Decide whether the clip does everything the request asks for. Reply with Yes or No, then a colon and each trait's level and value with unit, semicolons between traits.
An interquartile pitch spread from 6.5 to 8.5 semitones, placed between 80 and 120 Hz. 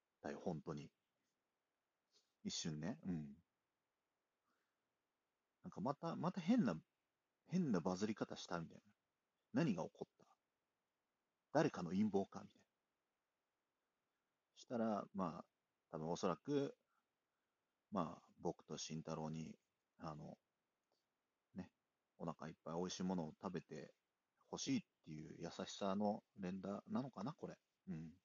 No: wide, 5.5 semitones; very low, 95 Hz